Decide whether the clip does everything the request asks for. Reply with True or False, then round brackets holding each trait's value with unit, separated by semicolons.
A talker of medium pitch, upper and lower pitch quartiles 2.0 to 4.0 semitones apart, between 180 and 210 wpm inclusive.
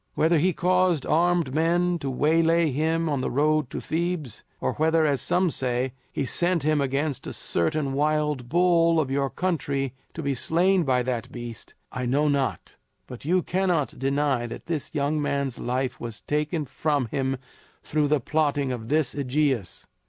False (150 Hz; 3.6 semitones; 170 wpm)